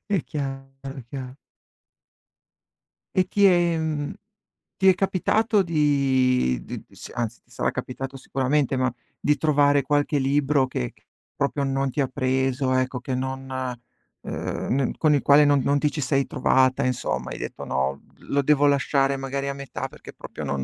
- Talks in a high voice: No, low, 135 Hz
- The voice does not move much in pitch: Yes, narrow, 2.1 semitones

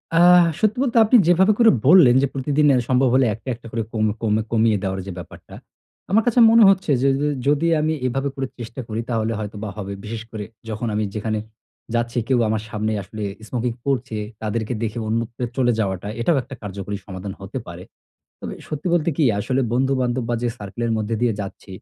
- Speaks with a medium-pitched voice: No, low, 120 Hz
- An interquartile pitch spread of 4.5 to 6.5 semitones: No, average, 4.1 semitones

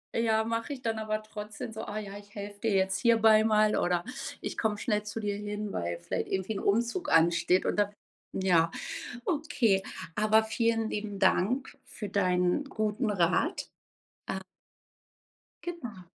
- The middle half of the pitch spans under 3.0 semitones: Yes, narrow, 2.6 semitones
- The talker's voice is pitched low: No, high, 210 Hz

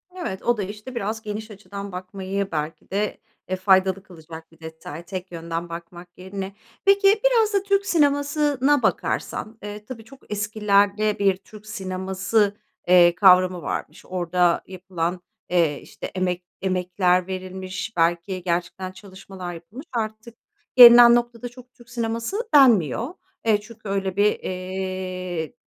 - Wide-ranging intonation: No, average, 3.8 semitones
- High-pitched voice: Yes, high, 195 Hz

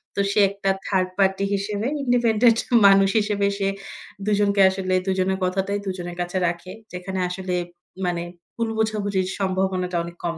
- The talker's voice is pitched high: Yes, high, 195 Hz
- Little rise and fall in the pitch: Yes, narrow, 1.7 semitones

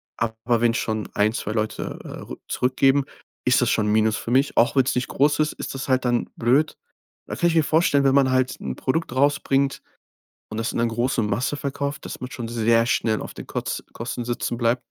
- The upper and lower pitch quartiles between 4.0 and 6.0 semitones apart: No, average, 3.1 semitones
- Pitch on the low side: Yes, low, 125 Hz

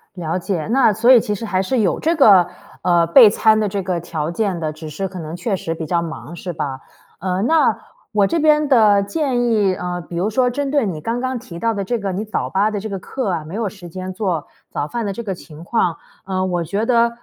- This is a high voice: Yes, high, 195 Hz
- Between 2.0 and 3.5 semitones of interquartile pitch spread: No, average, 4.8 semitones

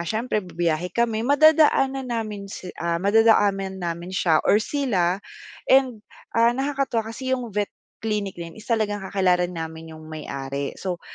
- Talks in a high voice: Yes, high, 205 Hz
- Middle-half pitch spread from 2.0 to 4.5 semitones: No, average, 5.1 semitones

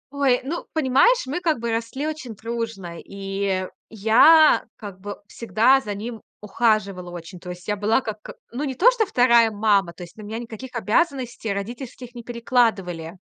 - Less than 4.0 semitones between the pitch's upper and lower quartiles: No, average, 4.5 semitones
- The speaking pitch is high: Yes, high, 225 Hz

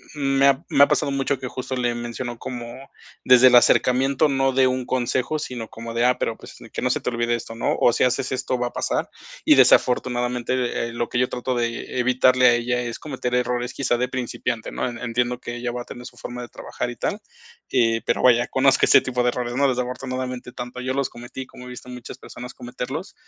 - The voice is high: No, low, 125 Hz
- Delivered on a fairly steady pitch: Yes, narrow, 1.2 semitones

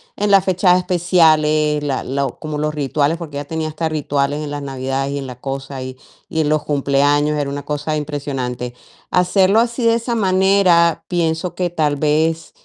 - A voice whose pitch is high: No, medium, 150 Hz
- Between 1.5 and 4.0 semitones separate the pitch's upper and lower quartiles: Yes, average, 3.6 semitones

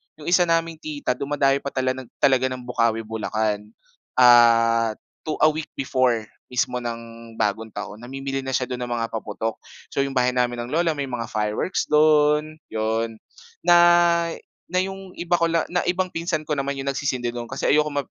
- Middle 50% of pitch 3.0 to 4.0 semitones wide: No, average, 4.9 semitones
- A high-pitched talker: No, low, 130 Hz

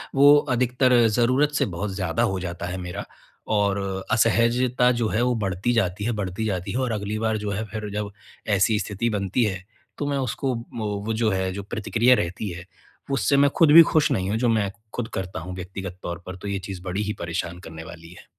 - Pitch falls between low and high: No, low, 105 Hz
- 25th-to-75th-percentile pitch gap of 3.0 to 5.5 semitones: Yes, average, 4.1 semitones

